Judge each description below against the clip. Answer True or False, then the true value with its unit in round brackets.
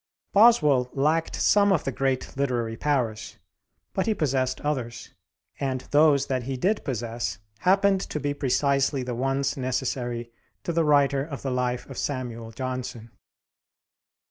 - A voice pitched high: False (135 Hz)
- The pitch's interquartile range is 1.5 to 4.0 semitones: True (2.9 semitones)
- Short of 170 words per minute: True (145 wpm)